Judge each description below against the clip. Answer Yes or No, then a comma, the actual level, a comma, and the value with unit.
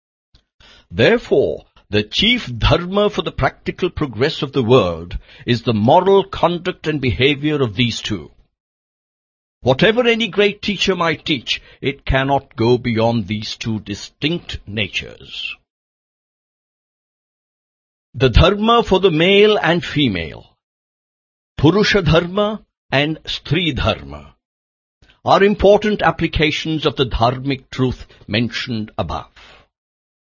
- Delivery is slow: Yes, slow, 110 wpm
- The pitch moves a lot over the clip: Yes, wide, 8.2 semitones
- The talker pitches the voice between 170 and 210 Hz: No, low, 135 Hz